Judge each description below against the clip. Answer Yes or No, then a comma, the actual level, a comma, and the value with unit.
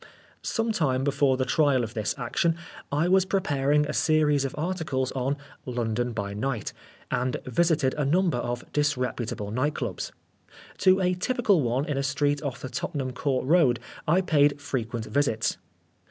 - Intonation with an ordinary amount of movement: Yes, average, 3.6 semitones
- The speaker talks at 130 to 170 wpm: Yes, average, 160 wpm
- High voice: No, medium, 140 Hz